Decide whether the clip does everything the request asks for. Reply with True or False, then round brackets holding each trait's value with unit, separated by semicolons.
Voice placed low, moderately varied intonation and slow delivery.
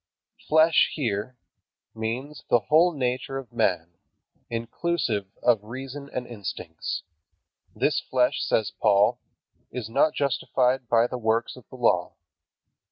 True (120 Hz; 3.4 semitones; 120 wpm)